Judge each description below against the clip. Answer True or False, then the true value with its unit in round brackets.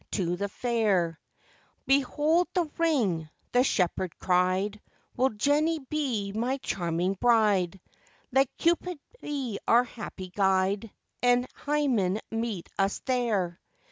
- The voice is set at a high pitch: True (225 Hz)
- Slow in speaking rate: True (100 wpm)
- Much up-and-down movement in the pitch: True (6.0 semitones)